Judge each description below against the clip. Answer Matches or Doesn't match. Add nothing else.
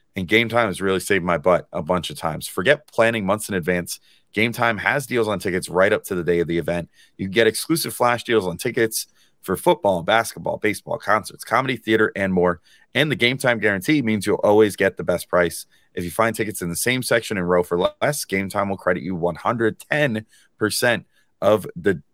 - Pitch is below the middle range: Matches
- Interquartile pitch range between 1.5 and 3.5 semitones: Doesn't match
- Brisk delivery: Matches